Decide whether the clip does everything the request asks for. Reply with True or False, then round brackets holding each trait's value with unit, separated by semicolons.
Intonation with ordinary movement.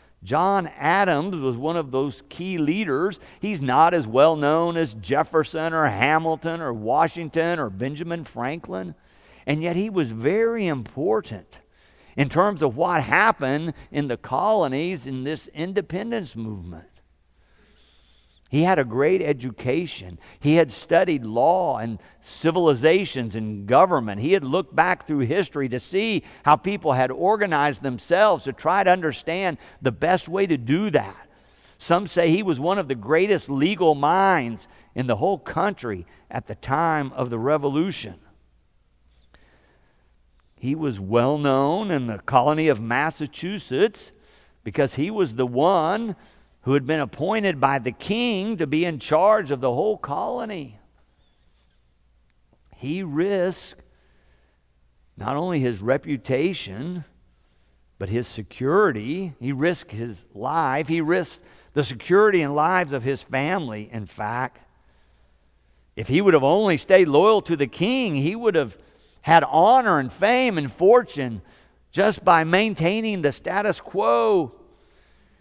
False (7.4 semitones)